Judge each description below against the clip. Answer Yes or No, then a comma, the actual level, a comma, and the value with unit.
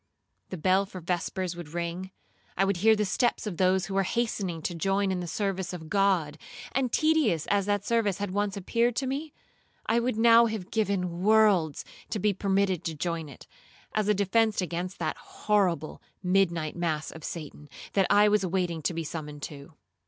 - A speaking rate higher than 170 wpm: Yes, average, 190 wpm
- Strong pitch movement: No, average, 3.6 semitones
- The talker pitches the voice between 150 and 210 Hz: Yes, high, 190 Hz